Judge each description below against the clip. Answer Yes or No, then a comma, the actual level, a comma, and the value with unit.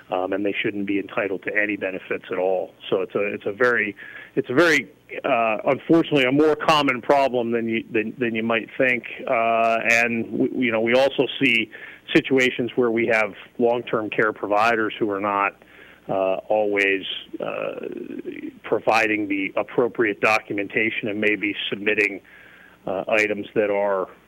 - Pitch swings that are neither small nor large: Yes, average, 4.7 semitones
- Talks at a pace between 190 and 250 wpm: No, average, 160 wpm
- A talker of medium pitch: No, low, 115 Hz